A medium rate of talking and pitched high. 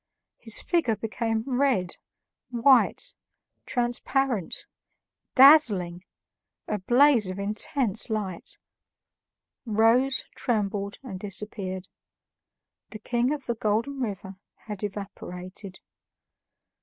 No: slow, 85 wpm; high, 220 Hz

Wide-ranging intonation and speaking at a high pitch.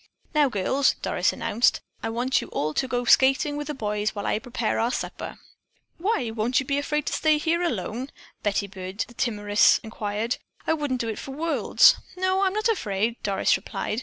Yes: wide, 5.7 semitones; high, 245 Hz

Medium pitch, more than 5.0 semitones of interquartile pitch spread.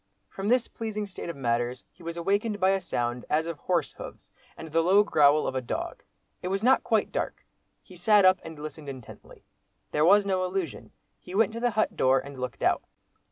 Yes: medium, 175 Hz; wide, 5.6 semitones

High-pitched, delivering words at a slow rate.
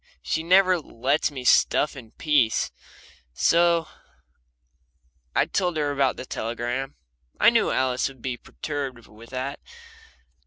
No: low, 135 Hz; slow, 125 wpm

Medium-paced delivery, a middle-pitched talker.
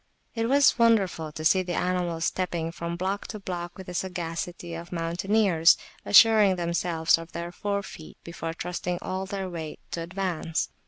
Yes: average, 160 wpm; medium, 175 Hz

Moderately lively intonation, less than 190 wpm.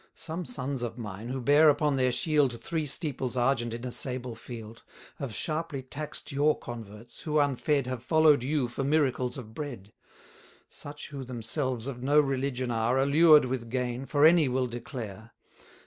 Yes: average, 3.4 semitones; average, 165 wpm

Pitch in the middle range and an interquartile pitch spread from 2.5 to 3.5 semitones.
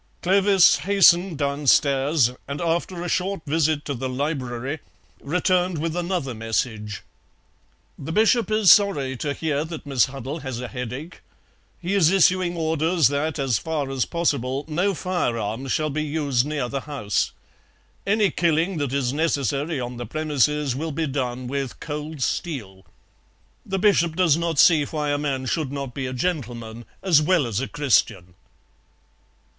No: medium, 150 Hz; average, 4.3 semitones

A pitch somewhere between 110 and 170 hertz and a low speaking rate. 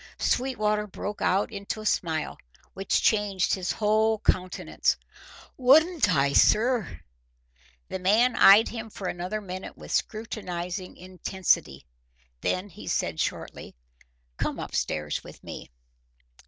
No: high, 200 Hz; slow, 120 wpm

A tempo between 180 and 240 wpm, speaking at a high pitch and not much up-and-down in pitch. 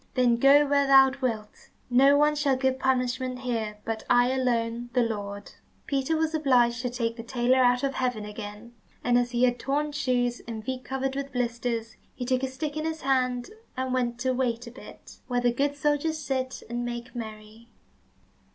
Yes: average, 190 wpm; very high, 250 Hz; narrow, 2.1 semitones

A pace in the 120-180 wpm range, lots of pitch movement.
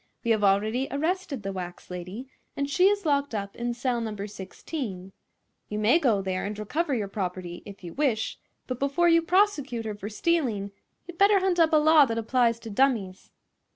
No: average, 190 wpm; wide, 6.9 semitones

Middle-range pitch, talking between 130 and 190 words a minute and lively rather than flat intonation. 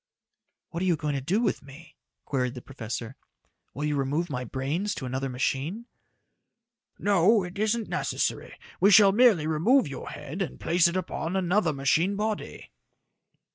Yes: medium, 165 Hz; average, 160 wpm; wide, 6.4 semitones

